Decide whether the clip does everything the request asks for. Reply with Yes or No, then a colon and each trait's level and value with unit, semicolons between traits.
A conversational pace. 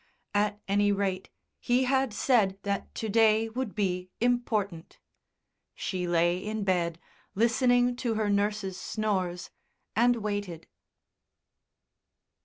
No: slow, 110 wpm